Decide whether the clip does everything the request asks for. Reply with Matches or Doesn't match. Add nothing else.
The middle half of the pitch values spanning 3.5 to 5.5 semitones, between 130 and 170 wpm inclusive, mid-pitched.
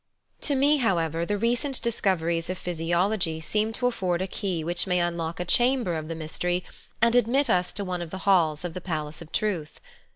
Doesn't match